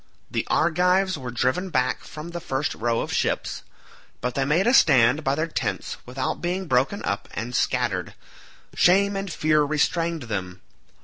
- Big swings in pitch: Yes, wide, 5.8 semitones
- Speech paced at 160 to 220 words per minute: Yes, average, 165 wpm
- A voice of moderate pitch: Yes, medium, 150 Hz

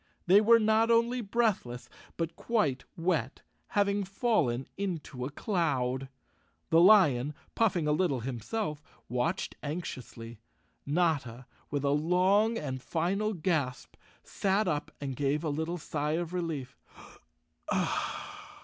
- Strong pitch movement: Yes, wide, 6.4 semitones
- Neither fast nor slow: No, slow, 120 wpm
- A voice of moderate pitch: Yes, medium, 165 Hz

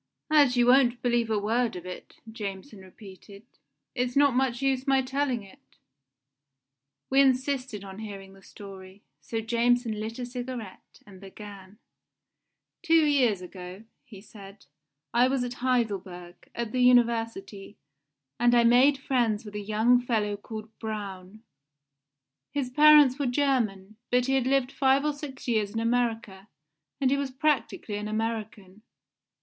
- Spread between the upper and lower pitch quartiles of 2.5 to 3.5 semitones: No, average, 4.0 semitones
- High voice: Yes, high, 230 Hz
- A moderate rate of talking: Yes, average, 145 wpm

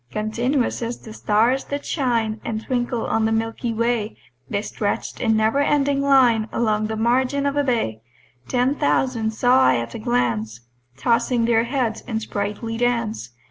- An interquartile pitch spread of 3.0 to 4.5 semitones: No, narrow, 2.6 semitones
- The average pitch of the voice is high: Yes, high, 230 Hz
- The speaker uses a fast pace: No, average, 165 wpm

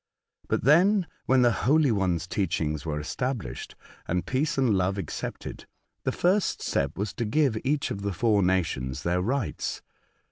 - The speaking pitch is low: Yes, low, 105 Hz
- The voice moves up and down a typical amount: No, wide, 7.0 semitones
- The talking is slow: No, average, 155 wpm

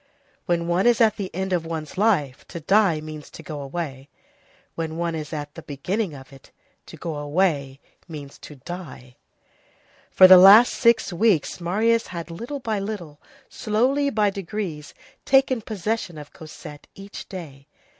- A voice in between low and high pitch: Yes, medium, 175 Hz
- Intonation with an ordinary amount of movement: No, wide, 5.7 semitones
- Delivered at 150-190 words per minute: Yes, average, 160 wpm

